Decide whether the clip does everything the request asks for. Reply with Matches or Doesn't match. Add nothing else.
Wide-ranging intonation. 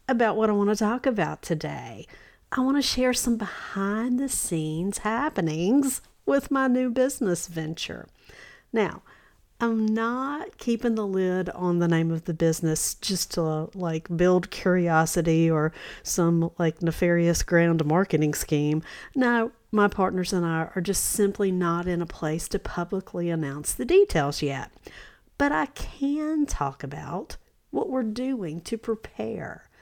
Matches